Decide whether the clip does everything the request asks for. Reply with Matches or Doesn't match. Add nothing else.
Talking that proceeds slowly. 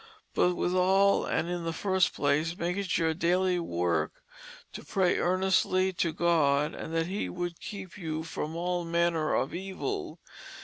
Doesn't match